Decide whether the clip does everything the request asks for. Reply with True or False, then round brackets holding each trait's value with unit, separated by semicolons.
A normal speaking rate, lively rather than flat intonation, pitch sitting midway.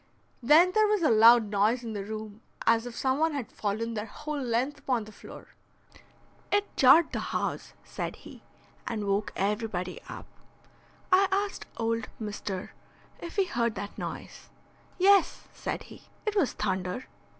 False (160 wpm; 6.5 semitones; 230 Hz)